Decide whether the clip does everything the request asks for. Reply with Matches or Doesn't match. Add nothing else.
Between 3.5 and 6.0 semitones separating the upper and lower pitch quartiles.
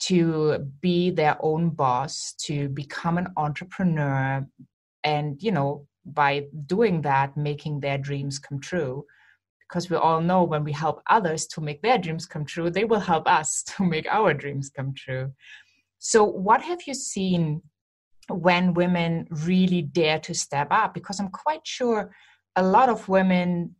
Matches